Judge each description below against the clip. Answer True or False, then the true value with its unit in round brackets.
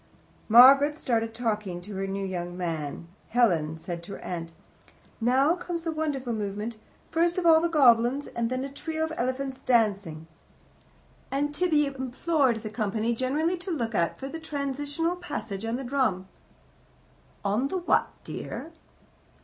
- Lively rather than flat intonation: True (6.0 semitones)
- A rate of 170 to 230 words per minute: False (155 wpm)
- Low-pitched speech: False (250 Hz)